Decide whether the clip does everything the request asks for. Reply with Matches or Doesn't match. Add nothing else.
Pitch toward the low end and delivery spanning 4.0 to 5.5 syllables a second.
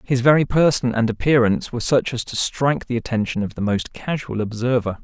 Doesn't match